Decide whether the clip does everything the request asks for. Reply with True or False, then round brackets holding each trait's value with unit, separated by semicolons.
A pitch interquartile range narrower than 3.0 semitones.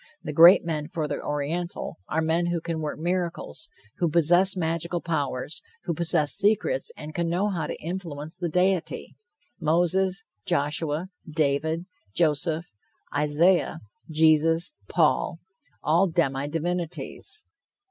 True (2.4 semitones)